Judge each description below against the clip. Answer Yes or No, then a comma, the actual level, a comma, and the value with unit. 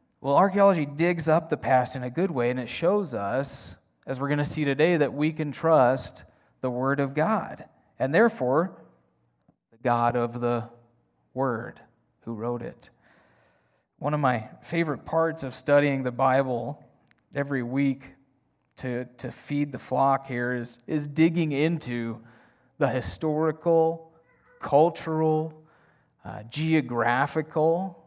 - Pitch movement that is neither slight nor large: Yes, average, 4.5 semitones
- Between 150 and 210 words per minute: No, slow, 135 wpm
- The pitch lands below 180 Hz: Yes, medium, 140 Hz